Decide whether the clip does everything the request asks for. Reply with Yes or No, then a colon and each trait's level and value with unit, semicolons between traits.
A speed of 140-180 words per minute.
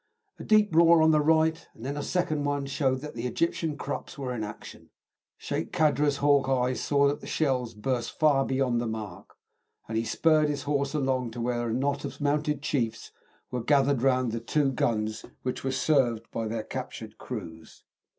No: average, 190 wpm